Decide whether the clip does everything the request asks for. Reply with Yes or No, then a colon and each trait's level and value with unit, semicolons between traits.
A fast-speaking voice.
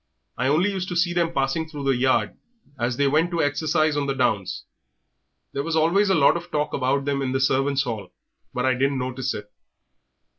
Yes: fast, 210 wpm